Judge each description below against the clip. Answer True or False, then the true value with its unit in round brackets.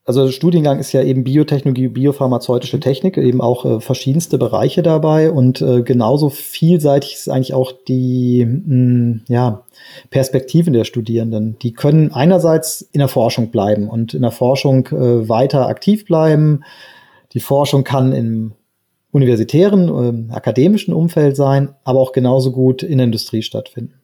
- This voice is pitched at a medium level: False (130 Hz)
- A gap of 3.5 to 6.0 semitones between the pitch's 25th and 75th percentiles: False (2.8 semitones)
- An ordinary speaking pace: True (150 wpm)